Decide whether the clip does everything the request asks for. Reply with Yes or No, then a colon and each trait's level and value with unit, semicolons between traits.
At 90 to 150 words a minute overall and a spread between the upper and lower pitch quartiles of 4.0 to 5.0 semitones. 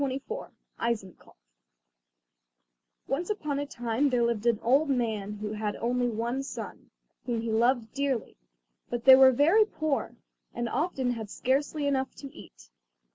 No: average, 145 wpm; average, 3.4 semitones